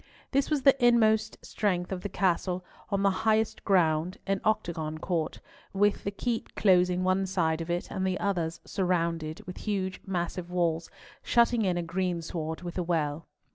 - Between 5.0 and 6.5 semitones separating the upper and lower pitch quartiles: No, average, 2.9 semitones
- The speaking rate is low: No, average, 170 wpm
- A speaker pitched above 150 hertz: Yes, medium, 185 Hz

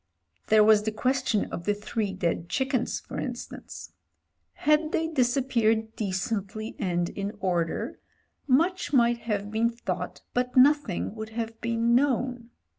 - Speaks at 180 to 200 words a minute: No, slow, 135 wpm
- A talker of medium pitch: No, high, 225 Hz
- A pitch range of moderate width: Yes, average, 3.4 semitones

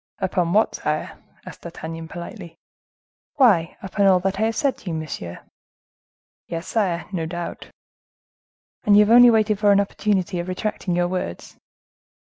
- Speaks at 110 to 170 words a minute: Yes, average, 155 wpm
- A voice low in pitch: No, medium, 185 Hz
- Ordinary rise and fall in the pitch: Yes, average, 3.6 semitones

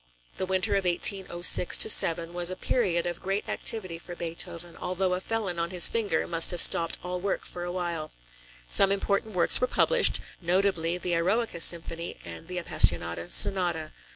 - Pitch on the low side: No, medium, 175 Hz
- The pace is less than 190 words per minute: Yes, average, 170 wpm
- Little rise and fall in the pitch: Yes, narrow, 2.2 semitones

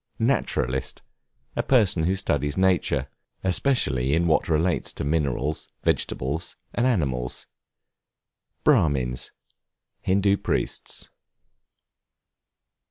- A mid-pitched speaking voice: No, very low, 80 Hz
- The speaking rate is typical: No, slow, 85 wpm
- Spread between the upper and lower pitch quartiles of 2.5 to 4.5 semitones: No, wide, 5.5 semitones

